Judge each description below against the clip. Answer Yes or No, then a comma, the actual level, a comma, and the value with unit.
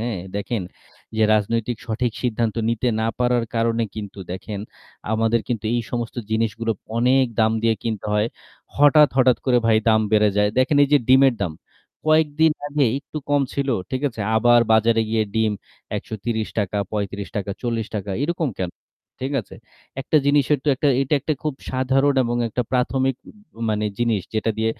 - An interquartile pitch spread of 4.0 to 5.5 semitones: No, average, 3.2 semitones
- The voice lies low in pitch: Yes, low, 115 Hz